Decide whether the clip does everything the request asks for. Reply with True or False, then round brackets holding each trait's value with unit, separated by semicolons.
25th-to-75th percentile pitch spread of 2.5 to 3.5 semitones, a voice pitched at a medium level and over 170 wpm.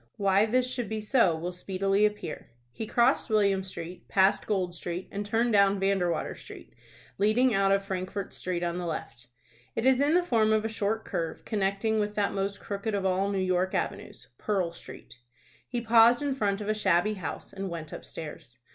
False (2.8 semitones; 200 Hz; 190 wpm)